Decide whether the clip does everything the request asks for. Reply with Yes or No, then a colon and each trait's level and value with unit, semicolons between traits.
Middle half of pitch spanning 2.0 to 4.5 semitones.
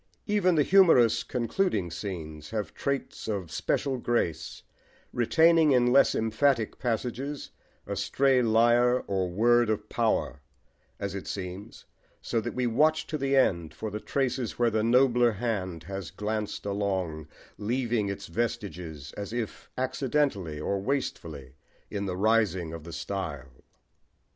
No: average, 4.9 semitones